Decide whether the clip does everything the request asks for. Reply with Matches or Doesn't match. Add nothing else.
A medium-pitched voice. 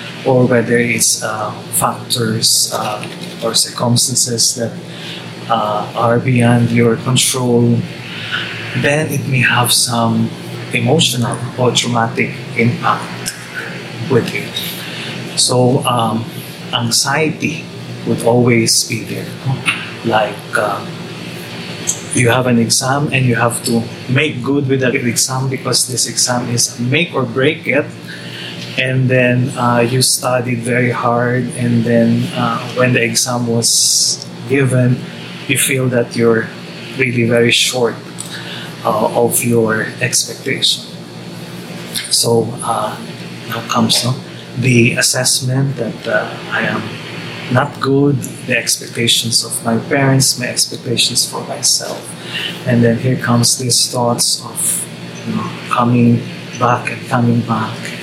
Doesn't match